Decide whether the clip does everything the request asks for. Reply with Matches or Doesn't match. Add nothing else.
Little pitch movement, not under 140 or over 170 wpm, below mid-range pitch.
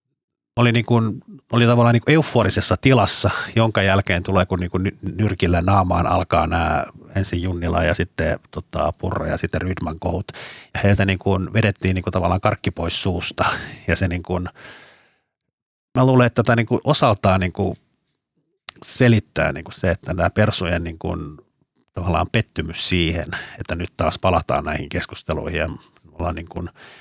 Doesn't match